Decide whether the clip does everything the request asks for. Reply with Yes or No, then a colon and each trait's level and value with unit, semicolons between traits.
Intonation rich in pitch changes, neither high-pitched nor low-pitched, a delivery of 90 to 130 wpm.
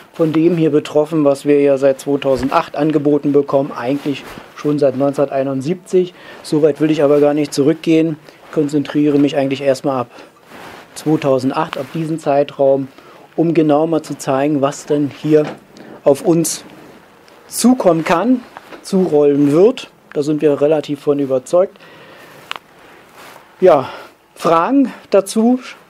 No: narrow, 2.5 semitones; medium, 150 Hz; slow, 125 wpm